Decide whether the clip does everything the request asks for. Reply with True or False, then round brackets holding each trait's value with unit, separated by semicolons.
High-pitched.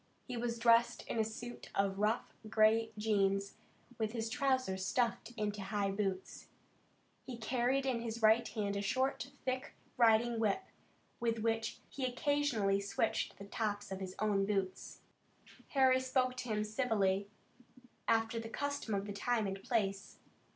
True (225 Hz)